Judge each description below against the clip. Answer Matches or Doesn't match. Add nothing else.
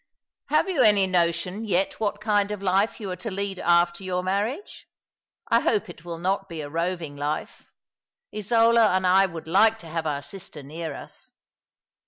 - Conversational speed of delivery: Matches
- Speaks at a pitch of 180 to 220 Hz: Matches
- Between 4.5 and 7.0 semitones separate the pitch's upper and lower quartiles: Doesn't match